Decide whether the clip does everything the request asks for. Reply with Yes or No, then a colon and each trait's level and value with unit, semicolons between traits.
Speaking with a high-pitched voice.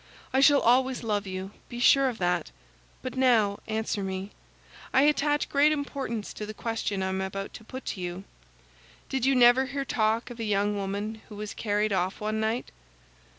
Yes: high, 220 Hz